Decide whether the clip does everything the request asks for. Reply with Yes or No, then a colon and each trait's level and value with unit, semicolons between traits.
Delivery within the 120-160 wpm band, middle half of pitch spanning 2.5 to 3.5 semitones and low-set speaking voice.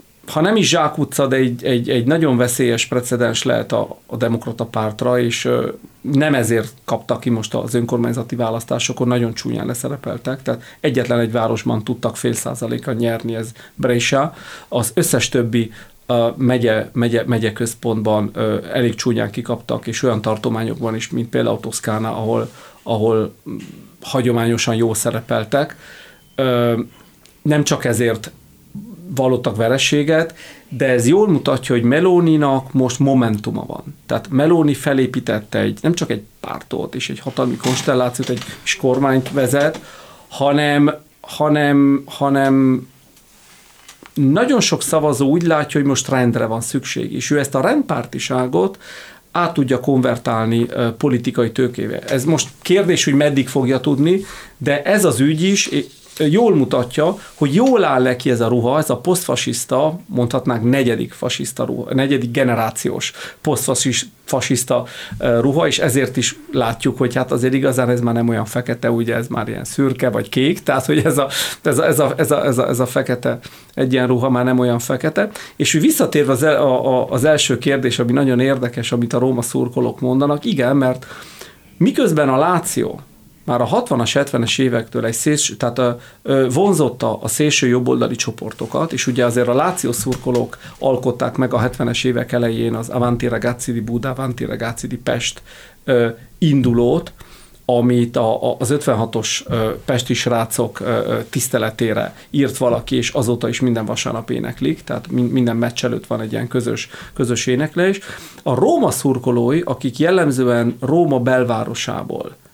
Yes: average, 145 wpm; average, 2.9 semitones; low, 125 Hz